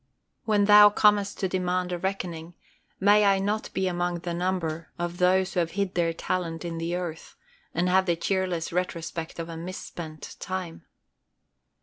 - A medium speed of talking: Yes, average, 165 wpm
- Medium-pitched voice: Yes, medium, 180 Hz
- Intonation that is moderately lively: No, narrow, 2.0 semitones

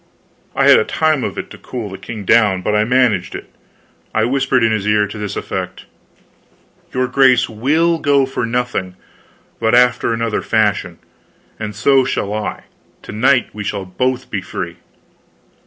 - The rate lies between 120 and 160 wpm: No, average, 170 wpm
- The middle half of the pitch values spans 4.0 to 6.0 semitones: No, average, 3.6 semitones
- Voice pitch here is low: Yes, low, 115 Hz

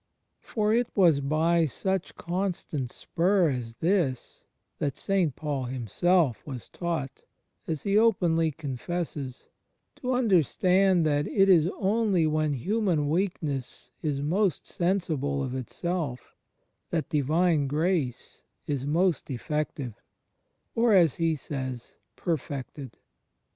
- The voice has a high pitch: No, medium, 160 Hz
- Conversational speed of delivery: No, slow, 115 wpm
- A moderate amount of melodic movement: Yes, average, 4.8 semitones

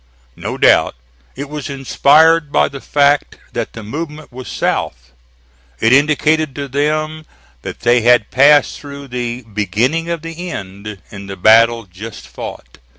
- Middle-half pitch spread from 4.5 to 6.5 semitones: Yes, average, 4.9 semitones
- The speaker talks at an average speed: Yes, average, 150 wpm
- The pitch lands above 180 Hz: No, medium, 140 Hz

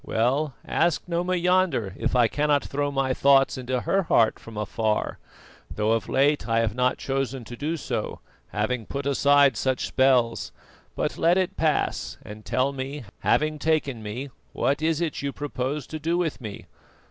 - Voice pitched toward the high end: No, low, 135 Hz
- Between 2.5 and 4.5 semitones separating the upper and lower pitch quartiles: Yes, average, 4.0 semitones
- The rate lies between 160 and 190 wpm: Yes, average, 170 wpm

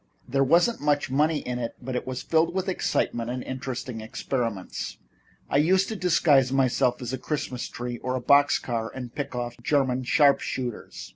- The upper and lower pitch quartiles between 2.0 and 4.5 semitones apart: Yes, average, 2.9 semitones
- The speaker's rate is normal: Yes, average, 185 wpm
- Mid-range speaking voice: No, low, 130 Hz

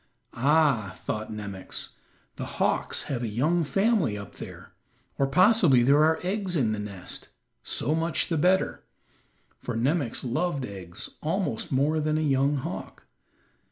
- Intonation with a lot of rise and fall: Yes, wide, 6.1 semitones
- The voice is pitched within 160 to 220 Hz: No, medium, 140 Hz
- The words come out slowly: No, average, 145 wpm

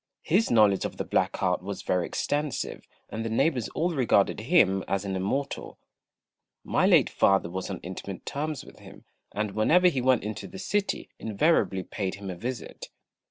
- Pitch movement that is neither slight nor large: No, wide, 7.1 semitones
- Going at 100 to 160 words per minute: No, average, 175 wpm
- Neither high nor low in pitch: No, low, 110 Hz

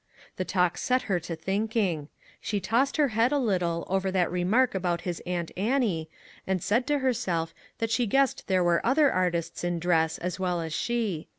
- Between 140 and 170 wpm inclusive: No, average, 190 wpm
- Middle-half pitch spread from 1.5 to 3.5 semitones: No, average, 5.2 semitones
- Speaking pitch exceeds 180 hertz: Yes, high, 190 Hz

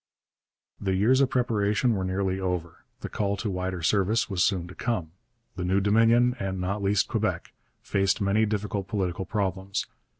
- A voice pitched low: Yes, low, 100 Hz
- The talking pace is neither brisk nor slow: Yes, average, 165 wpm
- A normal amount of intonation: No, narrow, 2.3 semitones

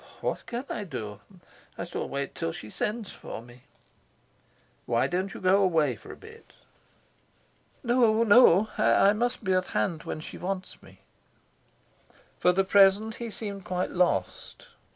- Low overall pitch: No, high, 190 Hz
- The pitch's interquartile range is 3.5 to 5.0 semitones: Yes, average, 4.3 semitones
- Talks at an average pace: Yes, average, 150 wpm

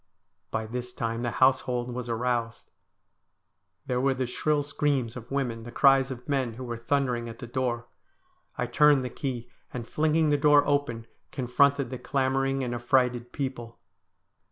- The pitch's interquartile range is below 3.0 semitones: Yes, narrow, 2.4 semitones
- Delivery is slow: No, average, 160 wpm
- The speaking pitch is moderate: No, low, 125 Hz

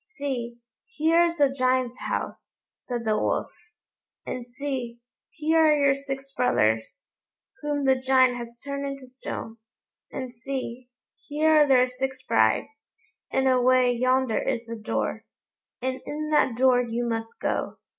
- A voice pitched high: Yes, very high, 260 Hz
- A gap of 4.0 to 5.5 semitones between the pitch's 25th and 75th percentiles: No, narrow, 2.6 semitones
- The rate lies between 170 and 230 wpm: No, average, 145 wpm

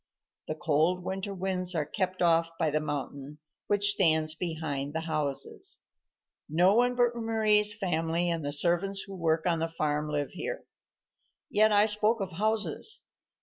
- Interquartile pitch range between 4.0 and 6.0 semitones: Yes, average, 4.6 semitones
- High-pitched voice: No, medium, 175 Hz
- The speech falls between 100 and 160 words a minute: Yes, average, 155 wpm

